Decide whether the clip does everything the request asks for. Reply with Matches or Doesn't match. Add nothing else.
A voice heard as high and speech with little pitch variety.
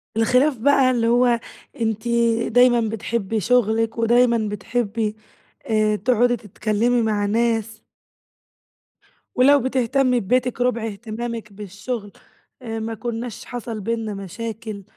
Matches